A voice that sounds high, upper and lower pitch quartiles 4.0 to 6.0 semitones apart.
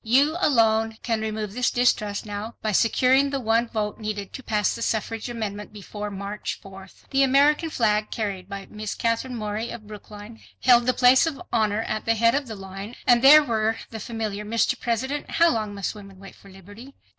No: high, 220 Hz; average, 2.7 semitones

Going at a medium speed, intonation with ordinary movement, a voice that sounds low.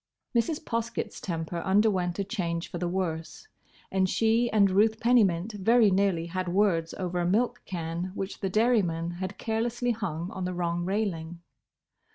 No: average, 165 wpm; average, 4.2 semitones; high, 190 Hz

